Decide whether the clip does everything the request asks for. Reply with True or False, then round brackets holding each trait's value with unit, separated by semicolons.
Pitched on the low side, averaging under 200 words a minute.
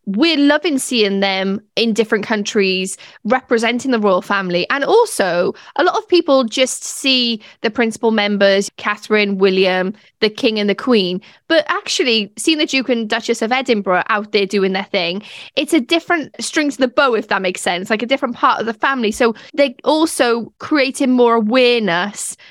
False (230 Hz; 180 wpm)